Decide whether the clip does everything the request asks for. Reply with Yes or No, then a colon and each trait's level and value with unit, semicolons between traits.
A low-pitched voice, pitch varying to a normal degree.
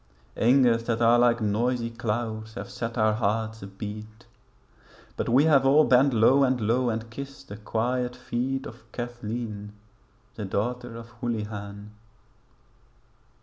No: low, 115 Hz; narrow, 2.3 semitones